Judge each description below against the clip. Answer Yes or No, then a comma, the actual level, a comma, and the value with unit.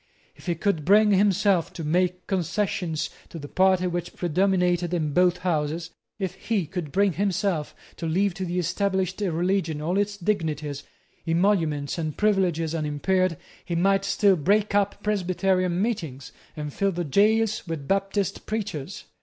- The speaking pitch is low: No, medium, 180 Hz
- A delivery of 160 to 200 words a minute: No, average, 150 wpm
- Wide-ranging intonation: No, average, 3.2 semitones